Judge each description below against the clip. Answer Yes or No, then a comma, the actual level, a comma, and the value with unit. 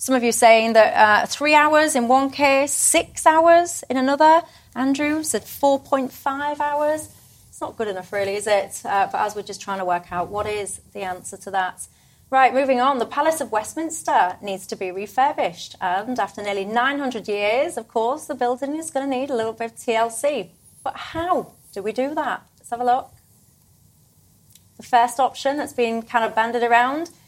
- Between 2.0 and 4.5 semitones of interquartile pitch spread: No, average, 5.0 semitones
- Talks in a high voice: Yes, high, 245 Hz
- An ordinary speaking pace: Yes, average, 195 wpm